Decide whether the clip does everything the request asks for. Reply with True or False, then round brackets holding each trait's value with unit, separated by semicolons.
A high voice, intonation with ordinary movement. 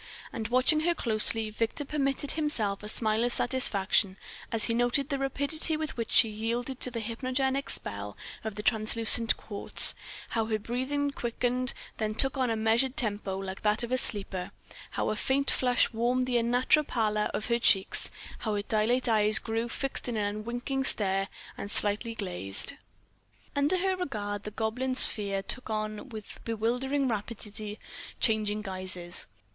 True (230 Hz; 3.4 semitones)